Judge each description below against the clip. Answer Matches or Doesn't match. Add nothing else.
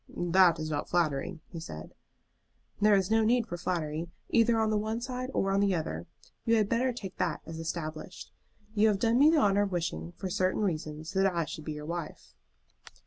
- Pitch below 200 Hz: Matches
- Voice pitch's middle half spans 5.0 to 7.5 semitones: Matches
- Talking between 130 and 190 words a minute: Doesn't match